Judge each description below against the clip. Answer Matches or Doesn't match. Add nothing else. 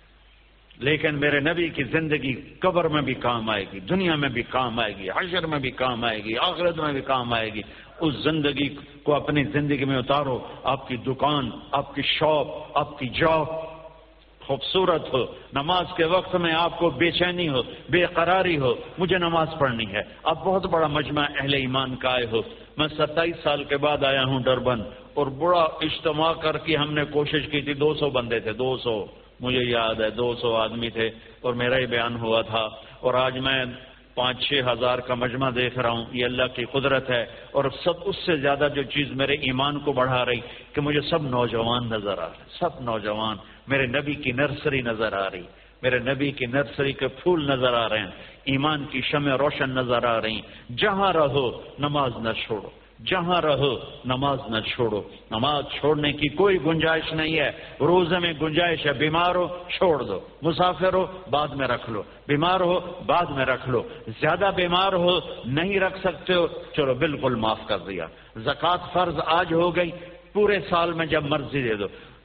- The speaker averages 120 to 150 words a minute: Doesn't match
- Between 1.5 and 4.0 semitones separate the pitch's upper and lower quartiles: Doesn't match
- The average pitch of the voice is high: Doesn't match